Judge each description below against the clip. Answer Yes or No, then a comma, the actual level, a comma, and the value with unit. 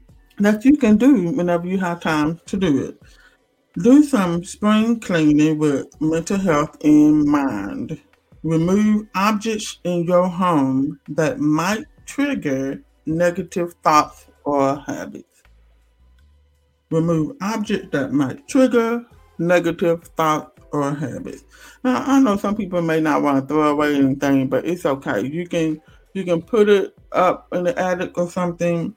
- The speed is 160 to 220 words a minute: No, average, 140 wpm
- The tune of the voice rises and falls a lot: Yes, wide, 6.1 semitones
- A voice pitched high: No, medium, 175 Hz